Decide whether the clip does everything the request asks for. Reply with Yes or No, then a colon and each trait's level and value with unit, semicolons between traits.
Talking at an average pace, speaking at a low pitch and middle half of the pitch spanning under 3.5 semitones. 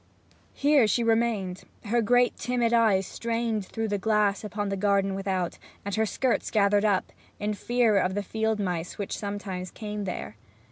No: average, 170 wpm; high, 210 Hz; narrow, 2.6 semitones